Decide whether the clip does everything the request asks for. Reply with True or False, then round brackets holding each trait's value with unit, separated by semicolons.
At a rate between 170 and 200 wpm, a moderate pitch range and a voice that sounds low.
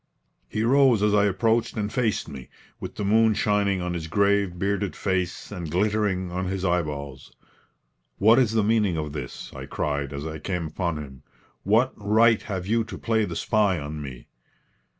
True (180 wpm; 4.9 semitones; 100 Hz)